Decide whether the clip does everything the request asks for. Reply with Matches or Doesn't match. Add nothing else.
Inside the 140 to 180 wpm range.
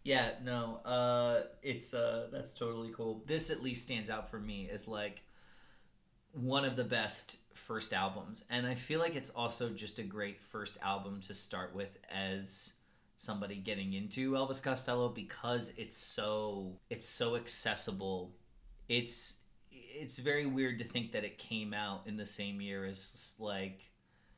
Matches